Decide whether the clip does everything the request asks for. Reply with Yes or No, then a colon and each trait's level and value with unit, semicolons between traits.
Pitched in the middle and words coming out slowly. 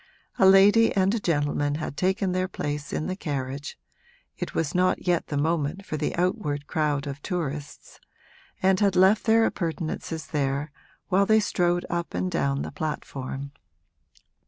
No: medium, 165 Hz; average, 160 wpm